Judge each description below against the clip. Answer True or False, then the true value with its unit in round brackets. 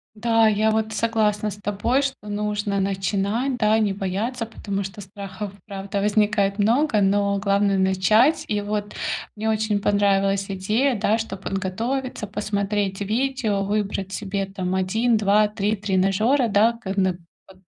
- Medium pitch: False (205 Hz)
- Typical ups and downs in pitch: False (2.0 semitones)